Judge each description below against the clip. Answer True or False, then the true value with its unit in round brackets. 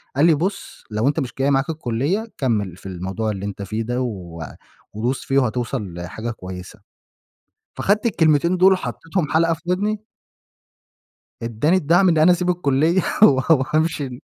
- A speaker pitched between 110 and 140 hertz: True (135 Hz)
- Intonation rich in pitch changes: True (7.4 semitones)